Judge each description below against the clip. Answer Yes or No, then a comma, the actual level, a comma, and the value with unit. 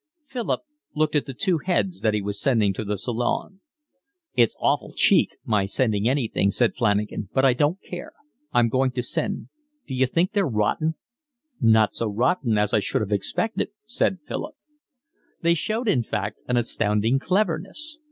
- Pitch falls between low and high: No, low, 125 Hz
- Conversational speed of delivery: Yes, average, 165 wpm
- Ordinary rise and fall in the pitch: No, wide, 8.4 semitones